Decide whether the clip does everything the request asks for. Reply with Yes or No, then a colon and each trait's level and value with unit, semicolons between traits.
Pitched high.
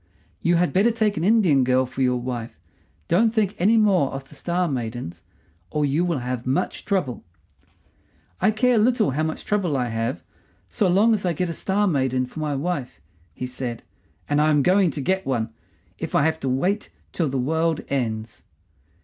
No: medium, 155 Hz